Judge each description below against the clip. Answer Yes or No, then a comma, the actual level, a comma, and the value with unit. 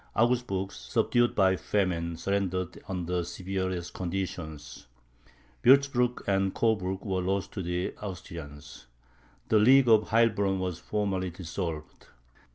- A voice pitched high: No, very low, 95 Hz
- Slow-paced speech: Yes, slow, 115 wpm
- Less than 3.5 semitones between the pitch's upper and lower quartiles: Yes, average, 2.9 semitones